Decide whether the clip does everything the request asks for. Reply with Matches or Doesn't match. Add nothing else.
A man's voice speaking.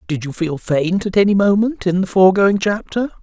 Matches